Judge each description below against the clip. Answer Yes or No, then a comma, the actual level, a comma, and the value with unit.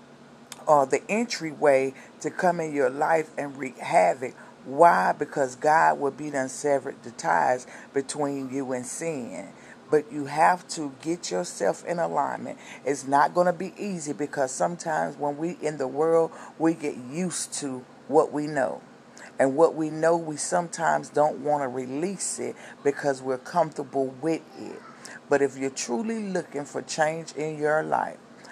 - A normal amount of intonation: Yes, average, 3.1 semitones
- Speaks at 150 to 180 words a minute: Yes, average, 160 wpm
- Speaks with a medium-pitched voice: Yes, medium, 150 Hz